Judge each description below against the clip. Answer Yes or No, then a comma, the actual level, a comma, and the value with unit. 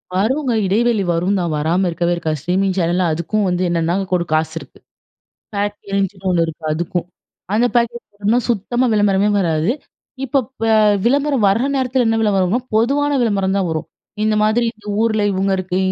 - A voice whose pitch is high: Yes, high, 195 Hz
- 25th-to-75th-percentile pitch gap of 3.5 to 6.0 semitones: Yes, average, 4.6 semitones